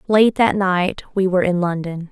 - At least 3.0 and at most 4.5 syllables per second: No, 4.9 syllables/s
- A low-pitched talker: No, medium, 185 Hz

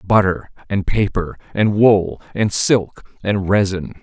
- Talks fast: No, slow, 135 wpm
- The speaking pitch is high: No, low, 100 Hz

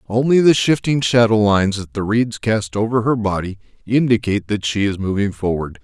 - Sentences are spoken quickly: No, average, 185 wpm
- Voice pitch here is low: Yes, low, 110 Hz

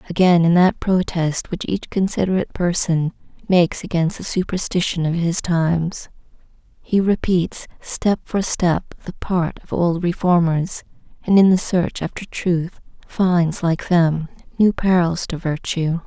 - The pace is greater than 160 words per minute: No, average, 140 wpm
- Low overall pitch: No, medium, 175 Hz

